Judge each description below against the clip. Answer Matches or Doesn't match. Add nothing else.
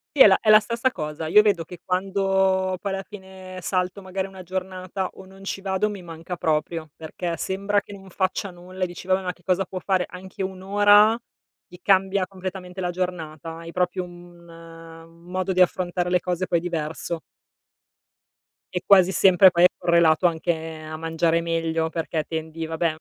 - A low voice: Doesn't match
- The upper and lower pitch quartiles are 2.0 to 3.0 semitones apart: Matches